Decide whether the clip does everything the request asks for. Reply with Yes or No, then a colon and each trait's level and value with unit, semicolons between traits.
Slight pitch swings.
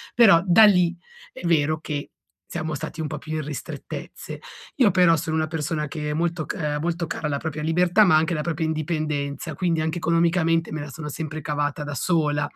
Yes: narrow, 2.1 semitones